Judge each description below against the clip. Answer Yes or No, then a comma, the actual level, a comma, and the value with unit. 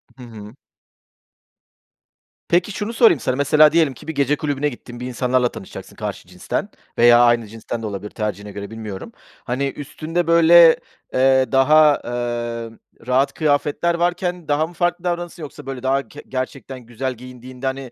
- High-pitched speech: No, low, 135 Hz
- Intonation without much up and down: No, average, 4.5 semitones